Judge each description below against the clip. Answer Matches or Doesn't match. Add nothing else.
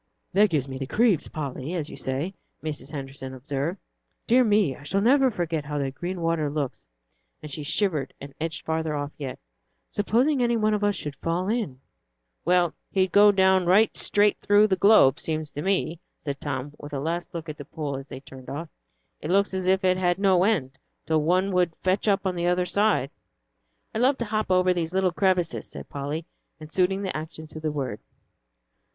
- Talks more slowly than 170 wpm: Doesn't match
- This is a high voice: Doesn't match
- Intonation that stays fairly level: Doesn't match